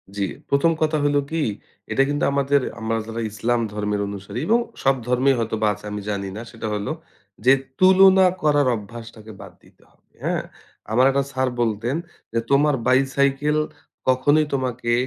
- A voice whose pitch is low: Yes, low, 130 Hz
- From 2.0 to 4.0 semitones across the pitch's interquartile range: No, average, 4.4 semitones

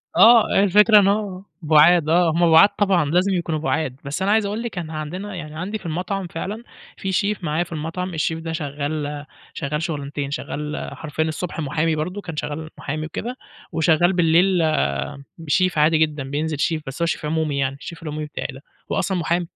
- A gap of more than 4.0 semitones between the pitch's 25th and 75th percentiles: No, average, 3.3 semitones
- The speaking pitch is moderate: Yes, medium, 165 Hz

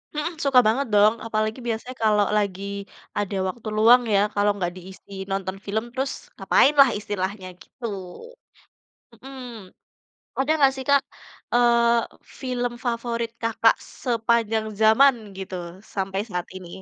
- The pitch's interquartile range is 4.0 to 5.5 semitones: No, average, 3.4 semitones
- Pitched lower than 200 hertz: No, high, 225 Hz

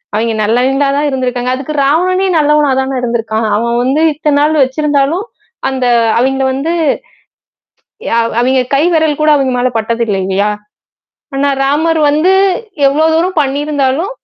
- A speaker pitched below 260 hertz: No, very high, 275 Hz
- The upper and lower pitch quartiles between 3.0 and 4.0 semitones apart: Yes, average, 3.4 semitones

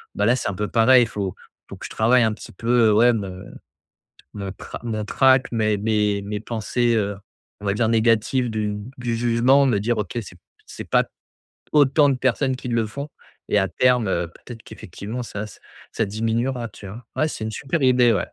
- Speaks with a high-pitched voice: No, low, 115 Hz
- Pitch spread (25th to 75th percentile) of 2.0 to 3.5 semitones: Yes, average, 2.9 semitones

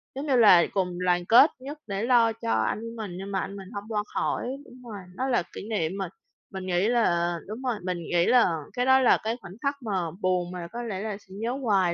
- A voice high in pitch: Yes, high, 200 Hz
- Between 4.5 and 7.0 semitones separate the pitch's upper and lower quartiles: Yes, average, 4.8 semitones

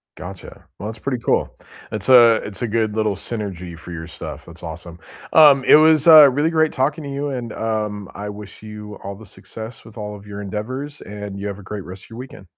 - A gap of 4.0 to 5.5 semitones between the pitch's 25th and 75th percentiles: Yes, average, 4.4 semitones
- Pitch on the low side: Yes, low, 105 Hz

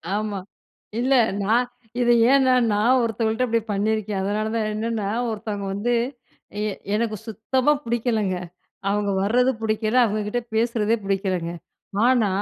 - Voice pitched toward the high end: Yes, high, 220 Hz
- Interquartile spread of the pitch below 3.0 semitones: Yes, narrow, 2.4 semitones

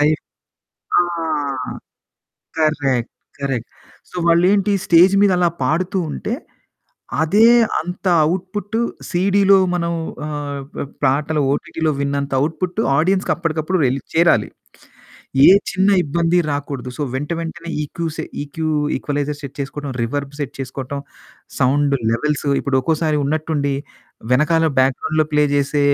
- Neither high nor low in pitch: Yes, medium, 155 Hz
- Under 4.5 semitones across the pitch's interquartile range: Yes, average, 3.4 semitones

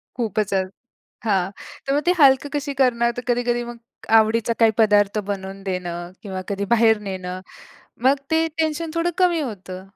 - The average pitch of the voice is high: Yes, high, 225 Hz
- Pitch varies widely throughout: Yes, wide, 5.8 semitones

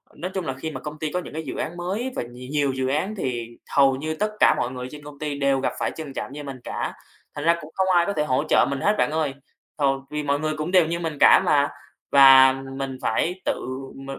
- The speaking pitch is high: No, medium, 145 Hz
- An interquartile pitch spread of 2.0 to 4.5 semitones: Yes, average, 3.3 semitones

